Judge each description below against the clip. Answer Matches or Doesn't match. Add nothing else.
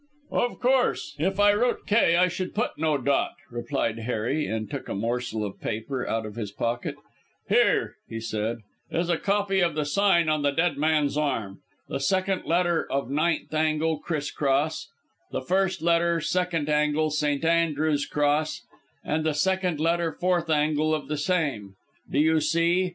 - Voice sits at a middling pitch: Matches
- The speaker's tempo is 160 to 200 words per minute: Matches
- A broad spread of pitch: Doesn't match